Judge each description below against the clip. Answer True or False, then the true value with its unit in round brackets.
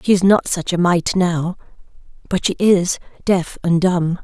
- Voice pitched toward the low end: False (180 Hz)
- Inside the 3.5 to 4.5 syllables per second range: True (4.2 syllables/s)